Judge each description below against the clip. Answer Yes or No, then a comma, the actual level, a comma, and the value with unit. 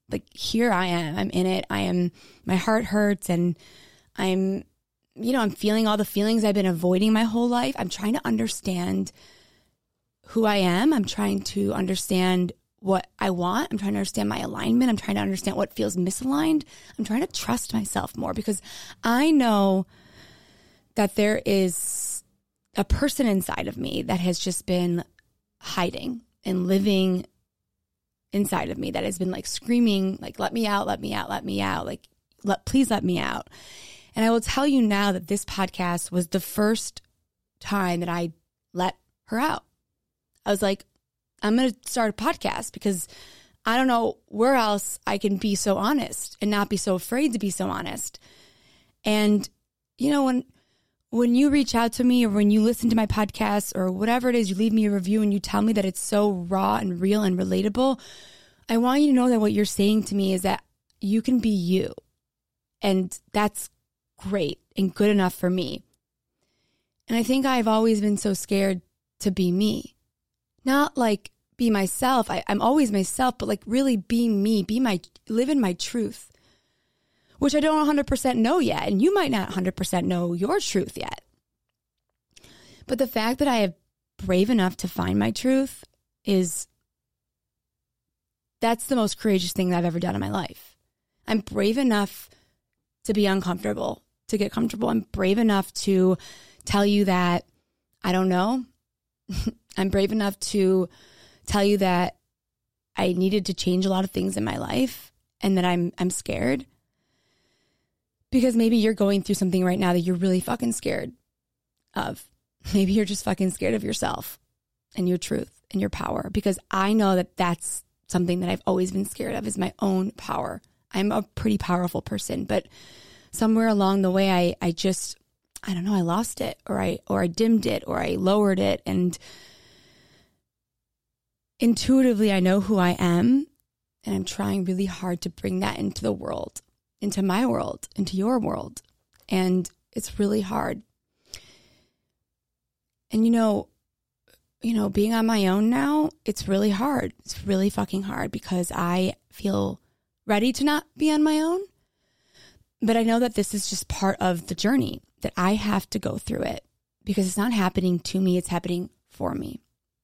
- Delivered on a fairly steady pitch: No, average, 3.7 semitones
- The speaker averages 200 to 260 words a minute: No, average, 180 wpm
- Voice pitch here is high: Yes, high, 200 Hz